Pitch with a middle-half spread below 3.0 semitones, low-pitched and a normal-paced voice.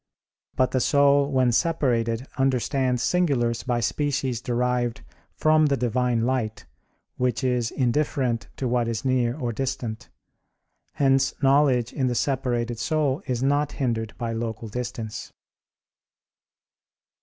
No: narrow, 2.5 semitones; low, 125 Hz; slow, 120 wpm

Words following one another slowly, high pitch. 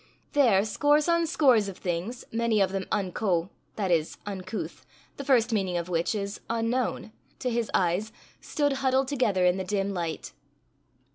No: average, 160 wpm; high, 210 Hz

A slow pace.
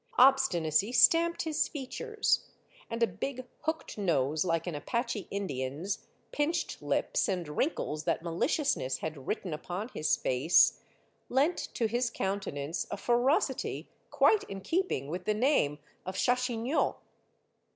Yes: slow, 130 wpm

